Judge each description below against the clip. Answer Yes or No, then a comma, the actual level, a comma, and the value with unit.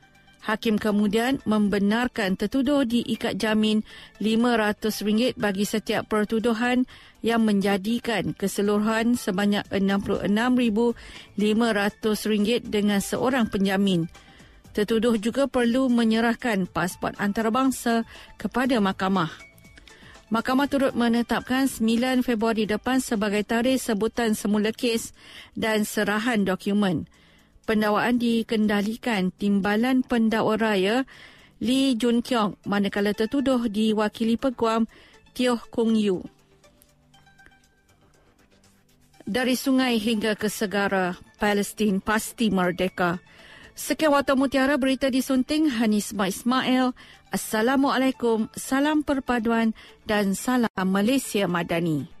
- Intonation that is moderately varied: Yes, average, 3.0 semitones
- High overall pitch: Yes, high, 220 Hz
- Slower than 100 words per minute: Yes, slow, 90 wpm